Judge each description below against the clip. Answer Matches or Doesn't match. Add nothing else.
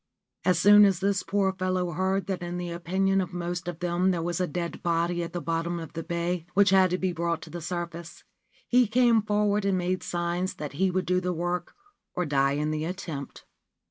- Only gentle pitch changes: Matches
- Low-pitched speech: Doesn't match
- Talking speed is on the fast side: Matches